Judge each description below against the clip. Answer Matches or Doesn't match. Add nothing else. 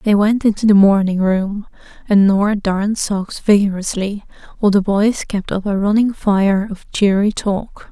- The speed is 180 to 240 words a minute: Doesn't match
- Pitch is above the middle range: Matches